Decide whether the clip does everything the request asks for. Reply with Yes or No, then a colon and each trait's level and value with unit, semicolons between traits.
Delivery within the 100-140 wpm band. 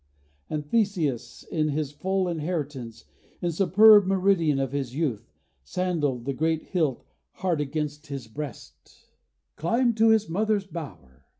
Yes: slow, 135 wpm